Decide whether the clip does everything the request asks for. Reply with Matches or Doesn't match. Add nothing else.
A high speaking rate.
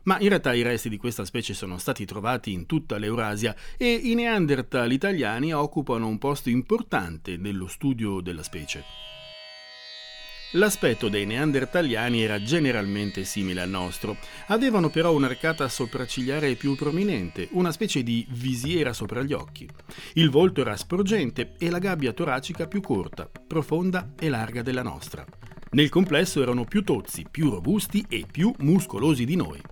Doesn't match